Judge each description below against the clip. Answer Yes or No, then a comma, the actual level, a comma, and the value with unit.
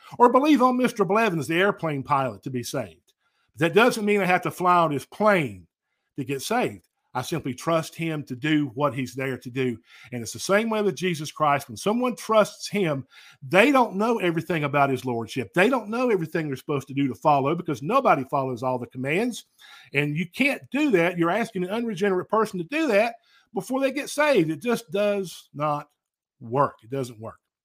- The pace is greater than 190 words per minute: Yes, fast, 205 wpm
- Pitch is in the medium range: Yes, medium, 165 Hz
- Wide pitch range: Yes, wide, 7.5 semitones